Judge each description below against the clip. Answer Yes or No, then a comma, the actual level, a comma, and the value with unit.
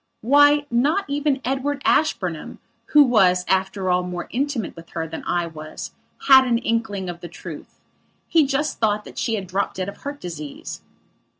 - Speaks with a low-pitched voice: No, high, 215 Hz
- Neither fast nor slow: Yes, average, 175 wpm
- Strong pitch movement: Yes, wide, 7.6 semitones